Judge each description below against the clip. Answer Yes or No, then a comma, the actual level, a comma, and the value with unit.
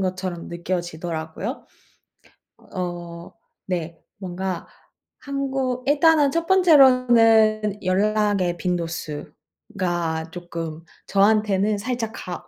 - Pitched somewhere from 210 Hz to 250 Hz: No, high, 190 Hz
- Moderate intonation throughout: Yes, average, 4.9 semitones